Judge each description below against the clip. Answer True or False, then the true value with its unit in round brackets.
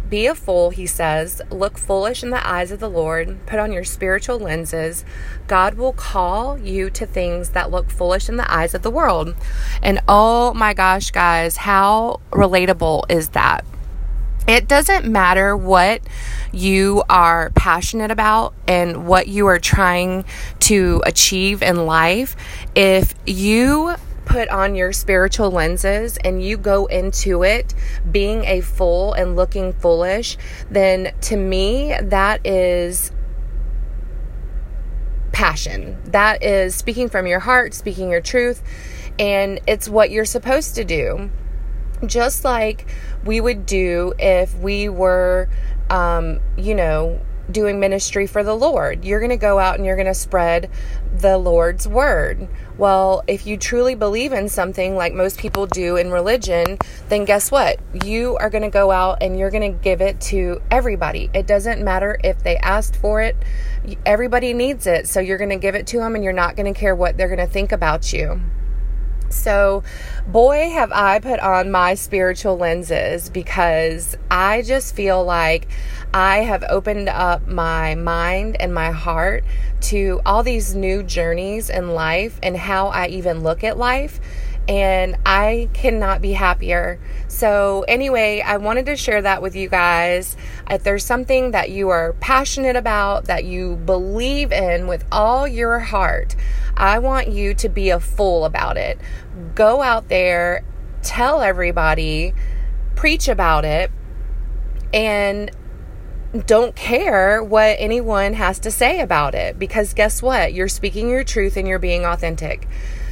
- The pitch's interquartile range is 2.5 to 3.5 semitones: True (3.1 semitones)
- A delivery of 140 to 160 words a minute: True (155 wpm)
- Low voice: False (195 Hz)